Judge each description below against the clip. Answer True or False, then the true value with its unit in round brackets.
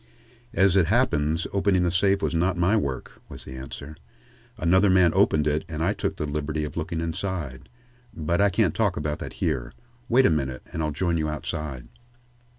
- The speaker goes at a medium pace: True (190 wpm)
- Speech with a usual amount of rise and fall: True (3.7 semitones)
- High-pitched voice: False (80 Hz)